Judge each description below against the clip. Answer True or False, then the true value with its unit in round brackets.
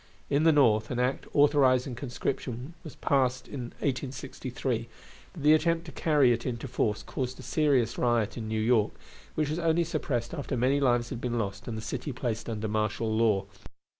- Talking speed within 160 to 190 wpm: True (185 wpm)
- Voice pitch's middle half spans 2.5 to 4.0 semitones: True (3.7 semitones)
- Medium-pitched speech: False (125 Hz)